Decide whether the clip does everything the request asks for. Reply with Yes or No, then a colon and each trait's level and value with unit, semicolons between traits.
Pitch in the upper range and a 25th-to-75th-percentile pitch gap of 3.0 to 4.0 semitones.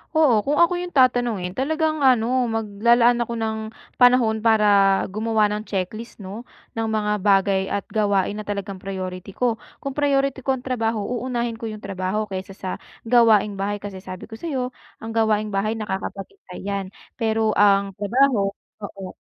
Yes: high, 220 Hz; average, 3.4 semitones